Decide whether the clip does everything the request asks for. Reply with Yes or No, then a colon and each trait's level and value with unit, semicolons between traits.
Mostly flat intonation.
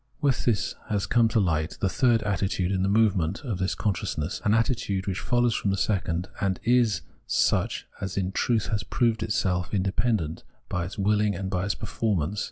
No: average, 3.1 semitones